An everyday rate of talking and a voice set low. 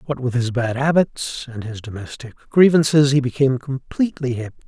Yes: average, 165 wpm; low, 130 Hz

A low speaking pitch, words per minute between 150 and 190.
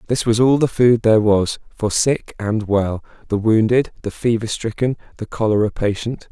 Yes: low, 110 Hz; average, 180 wpm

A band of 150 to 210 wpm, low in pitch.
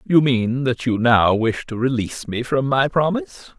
Yes: average, 200 wpm; low, 130 Hz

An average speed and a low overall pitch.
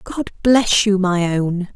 No: average, 170 wpm; high, 195 Hz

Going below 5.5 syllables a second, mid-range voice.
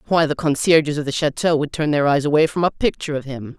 No: 6.5 syllables/s; medium, 150 Hz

